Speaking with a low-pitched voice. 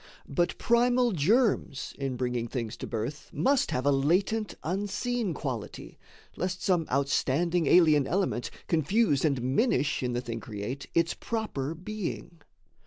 No: medium, 155 Hz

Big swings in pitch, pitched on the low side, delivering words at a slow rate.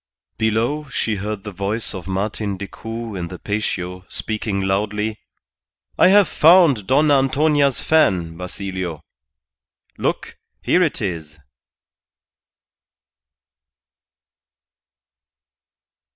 Yes: wide, 6.0 semitones; low, 105 Hz; slow, 90 wpm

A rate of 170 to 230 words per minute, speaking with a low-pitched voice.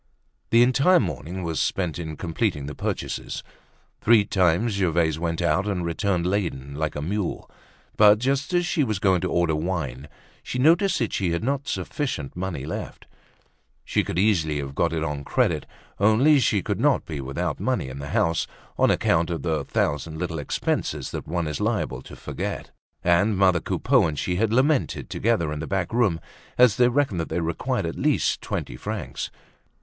Yes: average, 185 wpm; very low, 90 Hz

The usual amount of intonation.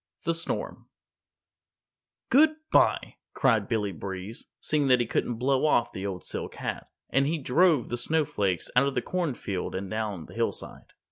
No: wide, 7.3 semitones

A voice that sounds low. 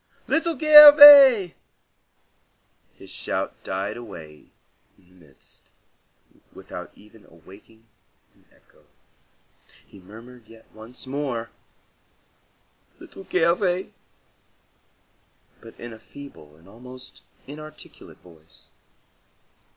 Yes: low, 120 Hz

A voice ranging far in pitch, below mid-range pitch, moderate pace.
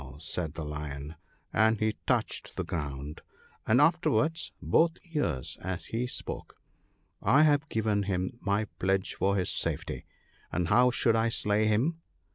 Yes: wide, 6.0 semitones; low, 105 Hz; average, 150 wpm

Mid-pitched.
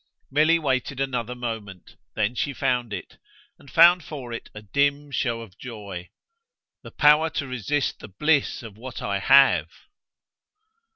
No: low, 125 Hz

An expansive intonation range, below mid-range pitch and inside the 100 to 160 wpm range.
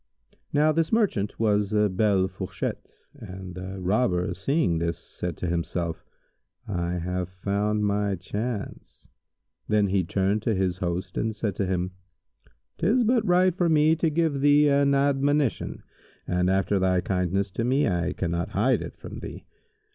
Yes: wide, 7.2 semitones; low, 100 Hz; average, 155 wpm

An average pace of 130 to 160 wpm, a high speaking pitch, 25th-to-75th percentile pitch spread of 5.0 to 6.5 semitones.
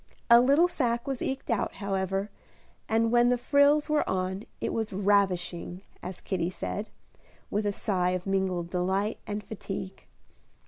No: average, 150 wpm; high, 200 Hz; average, 4.0 semitones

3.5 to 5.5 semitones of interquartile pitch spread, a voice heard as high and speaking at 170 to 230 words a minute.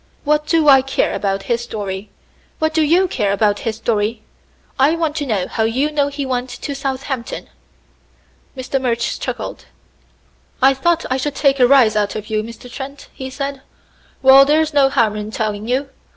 Yes: average, 4.4 semitones; very high, 260 Hz; average, 180 wpm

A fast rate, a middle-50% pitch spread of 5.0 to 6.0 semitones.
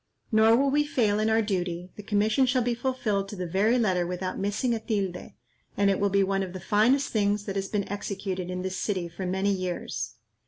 No: fast, 225 wpm; average, 2.9 semitones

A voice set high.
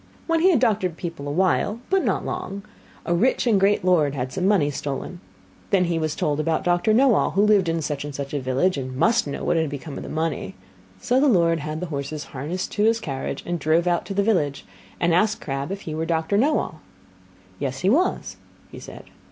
No: medium, 170 Hz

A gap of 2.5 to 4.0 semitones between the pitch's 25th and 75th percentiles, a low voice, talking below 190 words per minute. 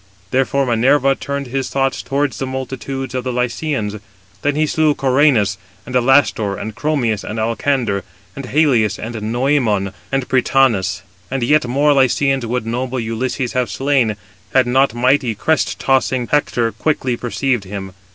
Yes: average, 3.0 semitones; low, 130 Hz; average, 150 wpm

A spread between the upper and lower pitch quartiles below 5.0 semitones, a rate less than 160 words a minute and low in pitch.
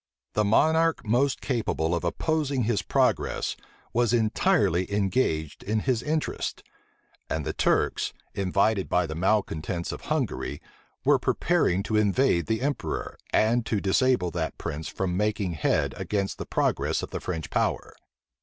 No: wide, 5.4 semitones; average, 145 wpm; low, 105 Hz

